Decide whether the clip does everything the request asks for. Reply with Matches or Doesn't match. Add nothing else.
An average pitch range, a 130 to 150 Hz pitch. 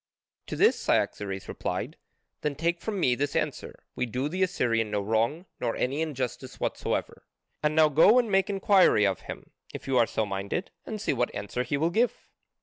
Doesn't match